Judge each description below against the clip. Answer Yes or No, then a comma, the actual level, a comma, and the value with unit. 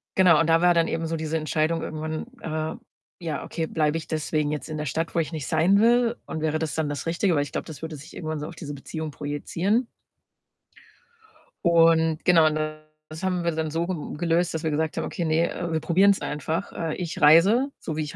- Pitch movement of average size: No, narrow, 1.5 semitones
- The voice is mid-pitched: Yes, medium, 160 Hz